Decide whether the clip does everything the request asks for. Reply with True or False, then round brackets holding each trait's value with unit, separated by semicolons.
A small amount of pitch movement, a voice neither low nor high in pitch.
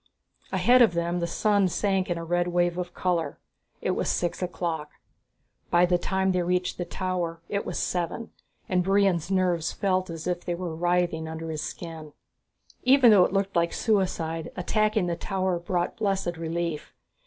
True (2.0 semitones; 175 Hz)